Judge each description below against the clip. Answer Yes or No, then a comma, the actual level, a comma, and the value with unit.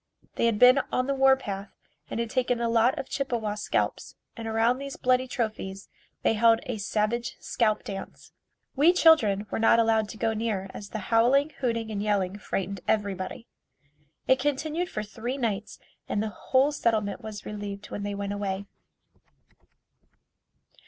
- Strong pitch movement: No, average, 3.6 semitones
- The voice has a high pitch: Yes, high, 225 Hz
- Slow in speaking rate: No, average, 165 wpm